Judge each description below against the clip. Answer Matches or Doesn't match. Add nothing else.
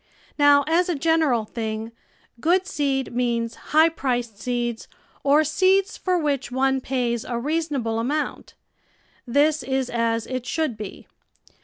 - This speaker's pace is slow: Doesn't match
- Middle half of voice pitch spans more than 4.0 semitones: Matches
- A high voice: Matches